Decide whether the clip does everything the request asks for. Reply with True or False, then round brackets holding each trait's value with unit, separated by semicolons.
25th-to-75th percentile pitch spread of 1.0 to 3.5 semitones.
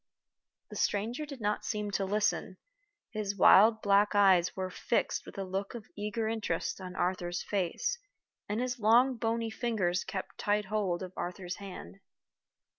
True (2.9 semitones)